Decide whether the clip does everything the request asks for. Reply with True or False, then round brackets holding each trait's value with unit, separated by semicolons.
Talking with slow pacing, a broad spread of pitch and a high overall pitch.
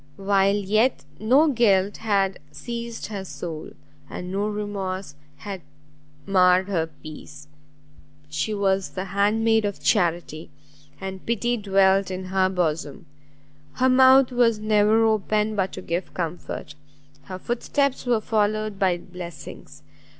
False (130 wpm; 3.0 semitones; 195 Hz)